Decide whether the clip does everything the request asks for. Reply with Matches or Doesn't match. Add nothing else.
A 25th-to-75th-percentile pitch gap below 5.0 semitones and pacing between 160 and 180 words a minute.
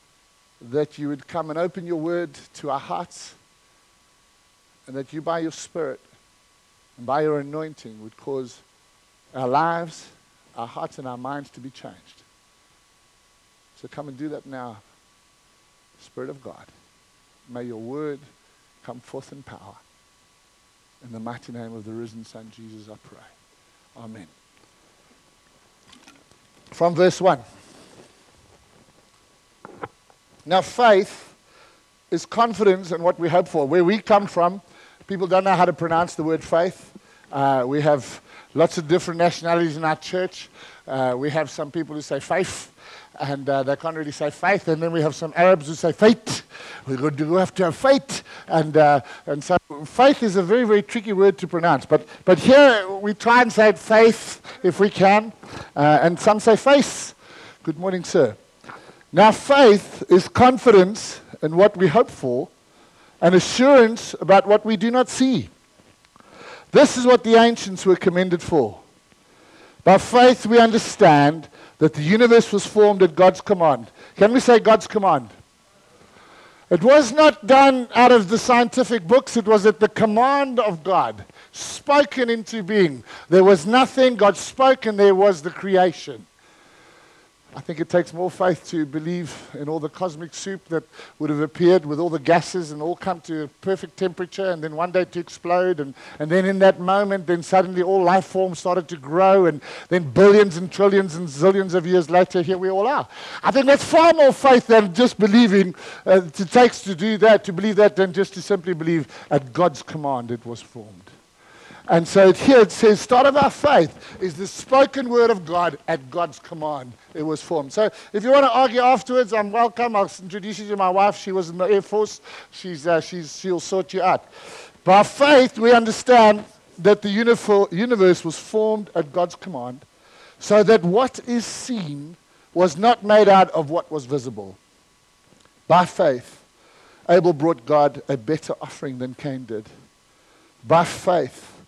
Doesn't match